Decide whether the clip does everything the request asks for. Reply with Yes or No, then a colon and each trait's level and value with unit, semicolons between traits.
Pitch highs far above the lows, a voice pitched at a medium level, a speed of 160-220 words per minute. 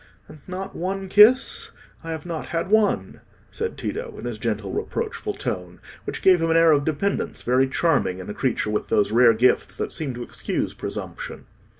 Yes: wide, 7.6 semitones; medium, 165 Hz; average, 190 wpm